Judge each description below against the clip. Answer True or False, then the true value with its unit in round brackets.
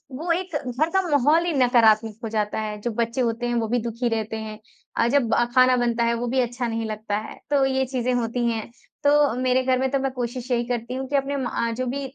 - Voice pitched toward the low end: False (245 Hz)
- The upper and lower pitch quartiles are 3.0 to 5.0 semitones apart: False (2.6 semitones)